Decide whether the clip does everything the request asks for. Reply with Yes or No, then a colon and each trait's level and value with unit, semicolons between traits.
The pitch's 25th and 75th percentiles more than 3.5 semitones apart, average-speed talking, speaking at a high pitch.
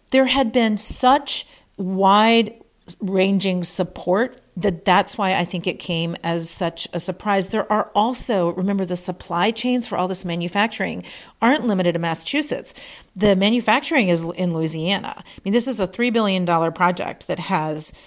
Yes: average, 4.2 semitones; average, 160 wpm; high, 195 Hz